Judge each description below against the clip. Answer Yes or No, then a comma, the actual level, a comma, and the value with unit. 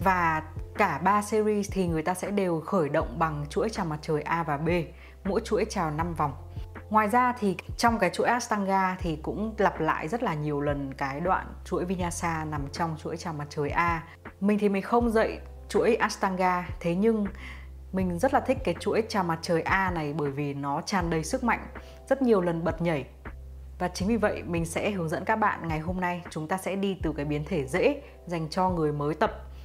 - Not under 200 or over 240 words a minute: Yes, average, 220 wpm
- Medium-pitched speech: Yes, medium, 175 Hz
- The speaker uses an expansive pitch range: No, average, 4.7 semitones